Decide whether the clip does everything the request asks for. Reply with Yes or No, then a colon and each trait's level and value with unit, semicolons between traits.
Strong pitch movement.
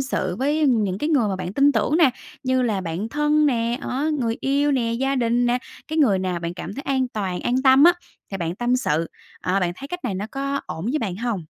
Yes: wide, 6.0 semitones